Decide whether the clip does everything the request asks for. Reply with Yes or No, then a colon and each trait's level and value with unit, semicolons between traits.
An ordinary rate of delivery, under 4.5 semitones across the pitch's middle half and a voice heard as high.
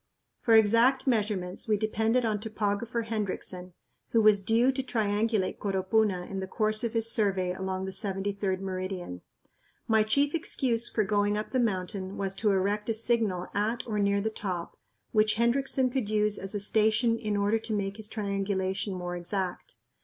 Yes: average, 170 wpm; narrow, 2.6 semitones; high, 210 Hz